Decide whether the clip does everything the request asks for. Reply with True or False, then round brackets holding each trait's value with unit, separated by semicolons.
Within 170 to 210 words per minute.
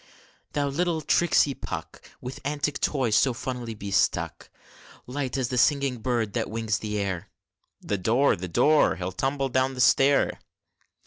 False (150 wpm)